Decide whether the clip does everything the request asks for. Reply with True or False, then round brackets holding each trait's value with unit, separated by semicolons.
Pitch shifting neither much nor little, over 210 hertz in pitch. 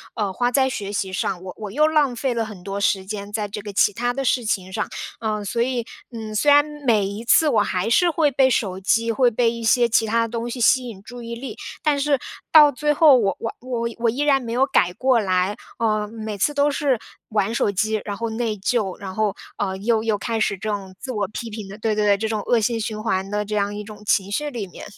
True (3.1 semitones; 225 Hz)